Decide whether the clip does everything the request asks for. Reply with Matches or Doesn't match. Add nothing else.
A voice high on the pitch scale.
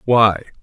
Doesn't match